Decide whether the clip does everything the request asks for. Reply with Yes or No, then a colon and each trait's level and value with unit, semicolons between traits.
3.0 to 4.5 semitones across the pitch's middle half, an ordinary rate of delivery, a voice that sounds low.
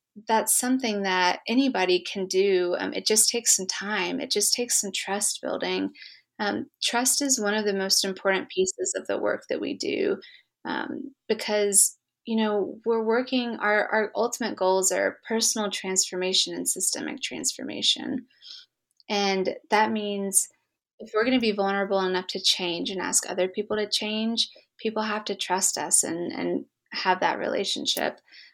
No: average, 3.5 semitones; average, 160 wpm; high, 210 Hz